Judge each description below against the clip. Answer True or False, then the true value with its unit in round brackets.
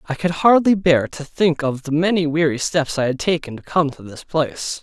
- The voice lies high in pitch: False (155 Hz)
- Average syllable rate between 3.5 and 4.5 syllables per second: False (5.1 syllables/s)